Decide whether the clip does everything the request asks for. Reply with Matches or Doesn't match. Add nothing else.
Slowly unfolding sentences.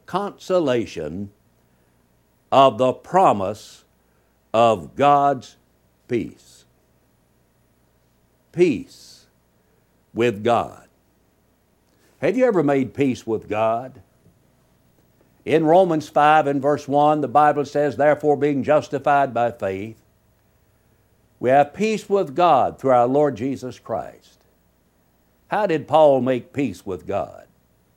Matches